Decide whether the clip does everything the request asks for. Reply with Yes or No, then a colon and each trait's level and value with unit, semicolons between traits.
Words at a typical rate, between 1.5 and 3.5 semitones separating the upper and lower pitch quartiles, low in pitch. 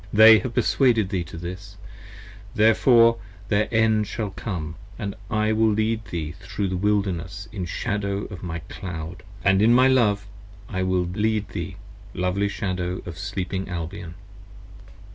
Yes: average, 150 wpm; average, 3.2 semitones; low, 100 Hz